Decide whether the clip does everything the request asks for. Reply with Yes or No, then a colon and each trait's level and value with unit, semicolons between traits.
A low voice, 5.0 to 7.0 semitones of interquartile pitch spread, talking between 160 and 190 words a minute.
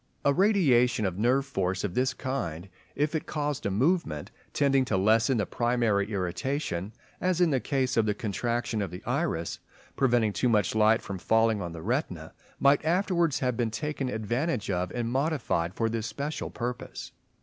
Yes: low, 120 Hz; average, 5.3 semitones; average, 175 wpm